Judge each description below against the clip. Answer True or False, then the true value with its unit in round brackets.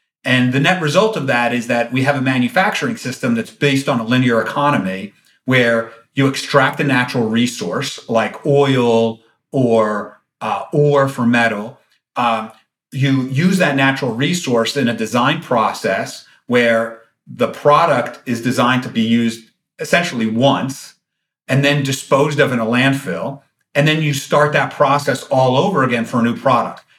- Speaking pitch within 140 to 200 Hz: False (130 Hz)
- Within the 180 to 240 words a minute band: False (160 wpm)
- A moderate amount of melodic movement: True (3.3 semitones)